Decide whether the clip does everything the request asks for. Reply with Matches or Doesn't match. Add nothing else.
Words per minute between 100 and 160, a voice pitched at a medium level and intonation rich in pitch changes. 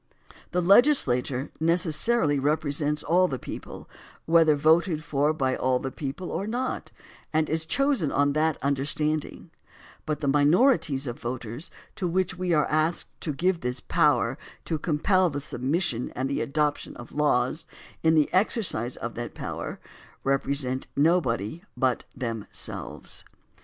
Doesn't match